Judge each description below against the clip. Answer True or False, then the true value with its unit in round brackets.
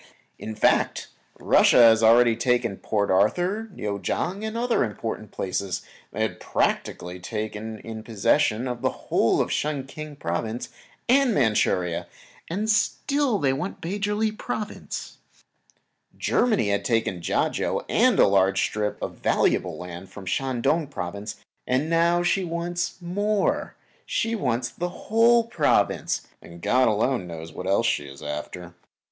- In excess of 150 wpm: False (140 wpm)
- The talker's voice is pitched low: True (120 Hz)